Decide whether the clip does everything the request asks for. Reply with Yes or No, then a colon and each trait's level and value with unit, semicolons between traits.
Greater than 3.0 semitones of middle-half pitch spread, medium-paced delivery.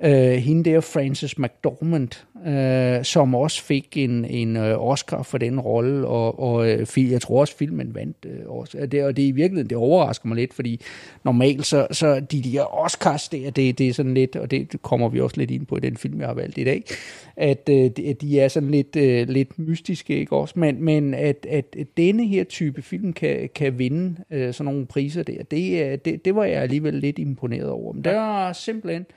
Yes: average, 3.8 semitones; average, 215 wpm